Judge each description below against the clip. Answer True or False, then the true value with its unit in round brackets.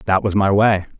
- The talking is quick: True (240 wpm)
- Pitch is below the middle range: True (100 Hz)